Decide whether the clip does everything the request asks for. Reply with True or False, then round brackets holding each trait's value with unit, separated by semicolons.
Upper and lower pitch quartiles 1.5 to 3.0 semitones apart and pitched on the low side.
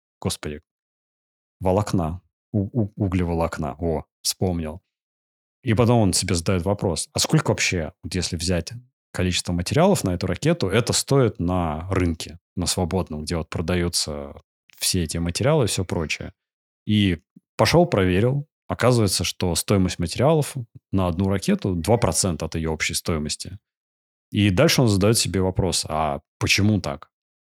False (4.1 semitones; 95 Hz)